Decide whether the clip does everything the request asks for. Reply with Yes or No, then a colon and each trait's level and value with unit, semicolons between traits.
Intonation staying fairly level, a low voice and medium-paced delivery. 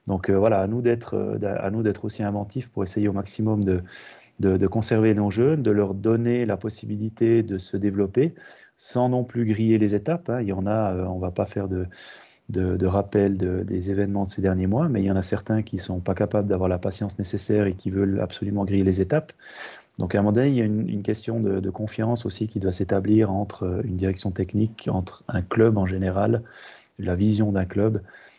No: narrow, 2.3 semitones; low, 100 Hz; fast, 230 wpm